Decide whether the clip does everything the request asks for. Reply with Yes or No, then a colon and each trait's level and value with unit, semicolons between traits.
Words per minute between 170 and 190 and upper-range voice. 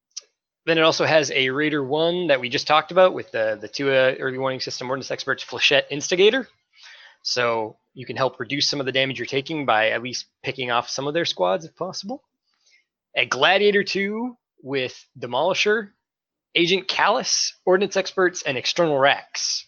No: average, 175 wpm; medium, 150 Hz